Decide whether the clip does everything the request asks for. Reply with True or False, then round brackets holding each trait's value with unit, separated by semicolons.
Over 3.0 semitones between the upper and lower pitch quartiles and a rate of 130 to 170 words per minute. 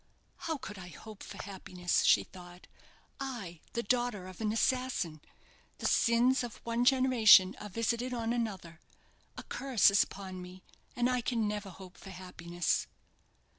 True (4.8 semitones; 155 wpm)